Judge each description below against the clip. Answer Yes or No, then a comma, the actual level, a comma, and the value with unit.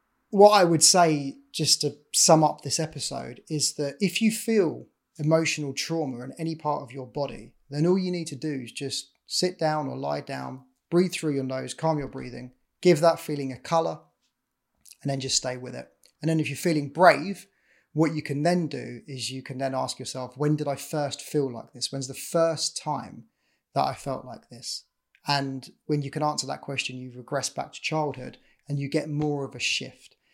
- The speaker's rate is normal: No, fast, 210 wpm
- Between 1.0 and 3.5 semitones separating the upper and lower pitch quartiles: Yes, average, 3.1 semitones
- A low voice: No, medium, 145 Hz